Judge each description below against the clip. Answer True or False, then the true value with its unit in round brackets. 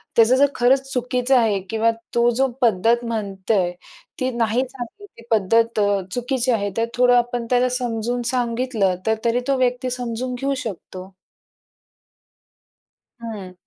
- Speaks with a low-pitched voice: False (240 Hz)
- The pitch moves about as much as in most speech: False (2.2 semitones)